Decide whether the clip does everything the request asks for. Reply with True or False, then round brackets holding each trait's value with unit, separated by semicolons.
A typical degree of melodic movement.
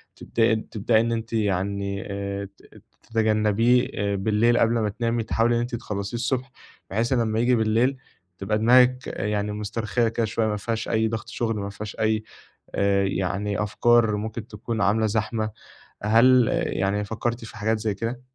False (2.1 semitones)